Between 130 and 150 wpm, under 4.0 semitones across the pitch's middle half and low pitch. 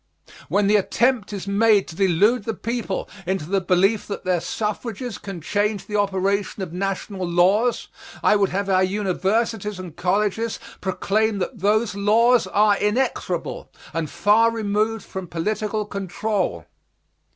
No: average, 140 wpm; narrow, 2.4 semitones; high, 200 Hz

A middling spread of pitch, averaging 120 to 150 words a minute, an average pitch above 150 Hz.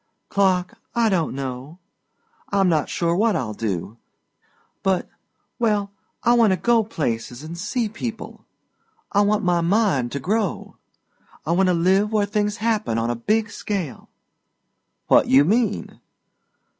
No: wide, 5.8 semitones; average, 145 wpm; high, 190 Hz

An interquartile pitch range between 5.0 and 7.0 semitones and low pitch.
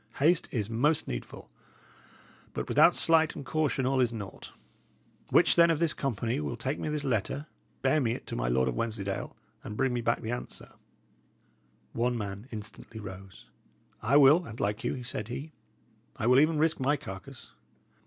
Yes: wide, 5.6 semitones; low, 120 Hz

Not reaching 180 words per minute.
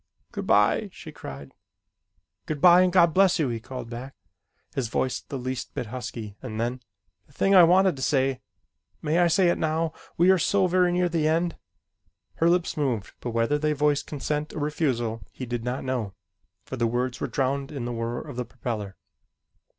No: average, 195 wpm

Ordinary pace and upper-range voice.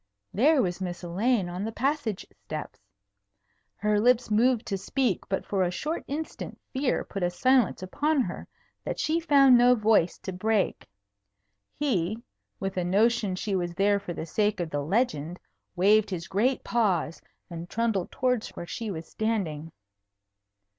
Yes: average, 160 wpm; high, 210 Hz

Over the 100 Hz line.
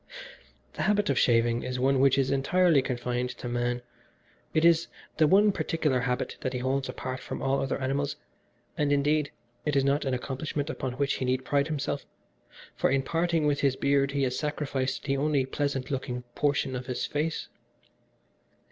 Yes: low, 135 Hz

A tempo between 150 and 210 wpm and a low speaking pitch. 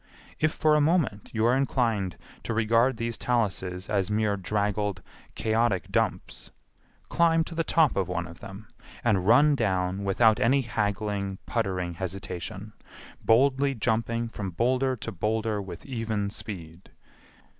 No: average, 140 wpm; low, 110 Hz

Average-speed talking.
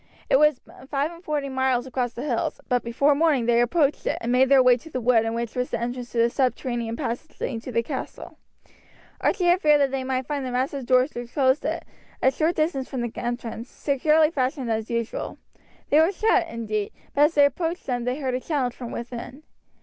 No: fast, 220 wpm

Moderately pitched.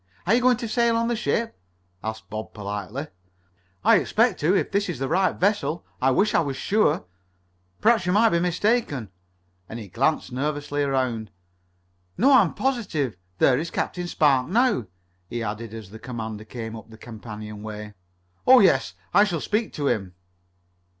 Yes: medium, 145 Hz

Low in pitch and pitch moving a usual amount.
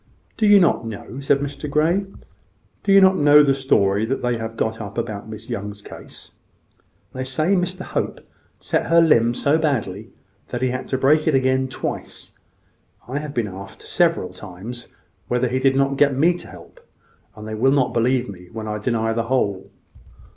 Yes: low, 130 Hz; average, 4.8 semitones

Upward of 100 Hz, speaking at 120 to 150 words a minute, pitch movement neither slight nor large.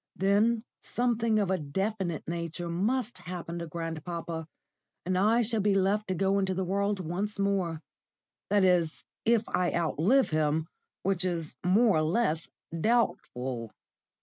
Yes: medium, 185 Hz; average, 145 wpm; average, 3.8 semitones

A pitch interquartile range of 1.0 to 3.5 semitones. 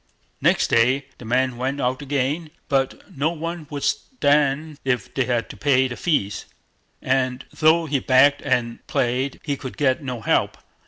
Yes: narrow, 2.5 semitones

